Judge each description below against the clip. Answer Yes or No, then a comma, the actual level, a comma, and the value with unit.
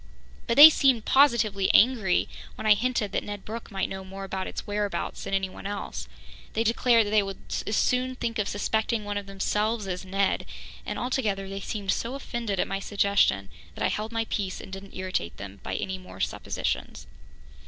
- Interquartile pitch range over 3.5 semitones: No, average, 2.9 semitones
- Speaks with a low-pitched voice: No, high, 205 Hz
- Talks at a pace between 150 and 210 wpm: Yes, average, 195 wpm